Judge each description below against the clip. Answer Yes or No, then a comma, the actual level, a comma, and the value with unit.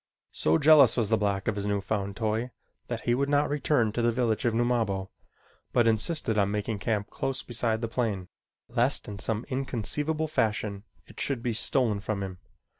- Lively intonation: No, average, 3.3 semitones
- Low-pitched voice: Yes, low, 115 Hz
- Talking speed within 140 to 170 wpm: No, average, 190 wpm